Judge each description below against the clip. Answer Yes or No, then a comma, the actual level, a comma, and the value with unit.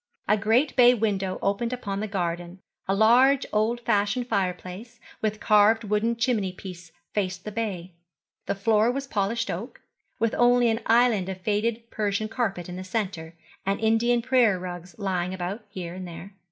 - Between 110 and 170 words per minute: Yes, average, 165 wpm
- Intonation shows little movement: No, average, 3.8 semitones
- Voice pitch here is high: Yes, high, 210 Hz